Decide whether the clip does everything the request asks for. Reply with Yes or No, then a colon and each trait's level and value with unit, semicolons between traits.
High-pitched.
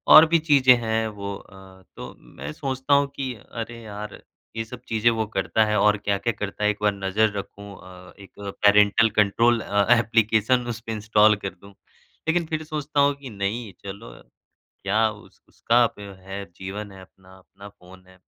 No: low, 105 Hz